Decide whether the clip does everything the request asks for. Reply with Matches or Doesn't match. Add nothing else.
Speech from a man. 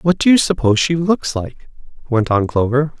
Matches